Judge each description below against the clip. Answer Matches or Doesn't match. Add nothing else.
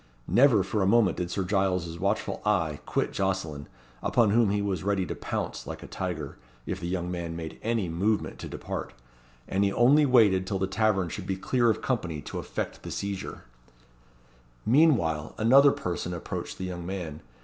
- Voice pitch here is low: Matches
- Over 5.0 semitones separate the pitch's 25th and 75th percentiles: Doesn't match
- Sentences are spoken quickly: Doesn't match